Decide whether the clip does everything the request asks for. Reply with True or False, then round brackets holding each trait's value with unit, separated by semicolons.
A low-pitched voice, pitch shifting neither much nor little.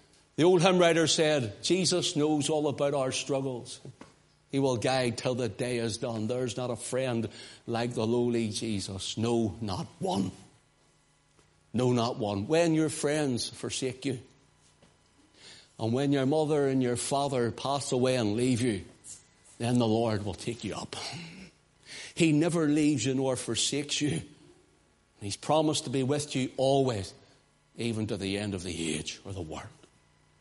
True (130 Hz; 3.9 semitones)